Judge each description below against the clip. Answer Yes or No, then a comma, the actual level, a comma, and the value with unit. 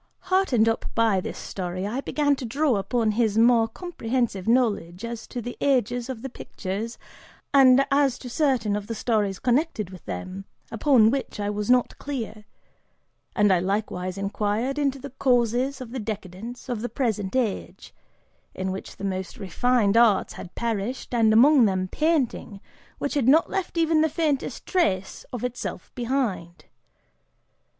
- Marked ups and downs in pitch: No, average, 4.4 semitones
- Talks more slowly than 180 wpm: Yes, average, 160 wpm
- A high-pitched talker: Yes, high, 235 Hz